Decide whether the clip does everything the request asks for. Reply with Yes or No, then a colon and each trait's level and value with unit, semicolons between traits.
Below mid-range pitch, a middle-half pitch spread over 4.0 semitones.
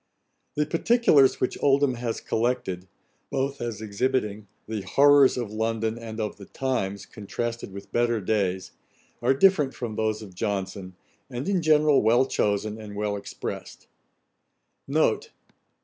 Yes: low, 115 Hz; average, 4.4 semitones